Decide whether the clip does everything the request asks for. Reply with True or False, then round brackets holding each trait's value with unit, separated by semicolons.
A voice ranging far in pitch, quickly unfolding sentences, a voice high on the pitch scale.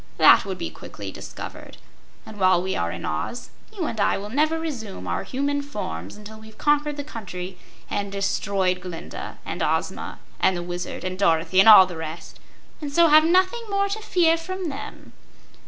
False (8.7 semitones; 185 wpm; 210 Hz)